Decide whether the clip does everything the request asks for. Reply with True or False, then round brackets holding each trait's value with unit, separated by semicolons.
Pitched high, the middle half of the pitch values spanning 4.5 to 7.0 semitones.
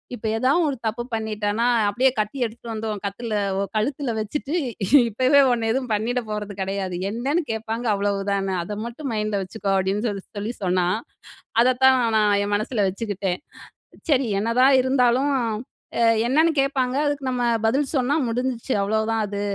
False (225 Hz; 3.9 semitones)